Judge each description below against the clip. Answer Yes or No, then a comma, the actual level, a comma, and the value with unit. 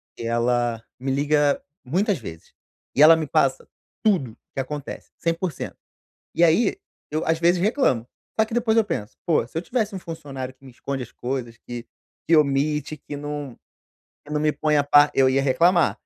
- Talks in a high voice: No, medium, 145 Hz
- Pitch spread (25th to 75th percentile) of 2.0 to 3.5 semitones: No, average, 4.2 semitones